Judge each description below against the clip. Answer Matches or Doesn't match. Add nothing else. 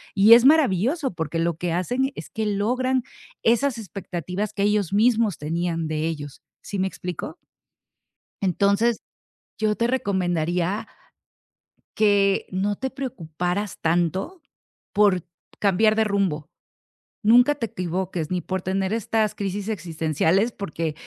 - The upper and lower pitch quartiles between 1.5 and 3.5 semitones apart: Doesn't match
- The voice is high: Matches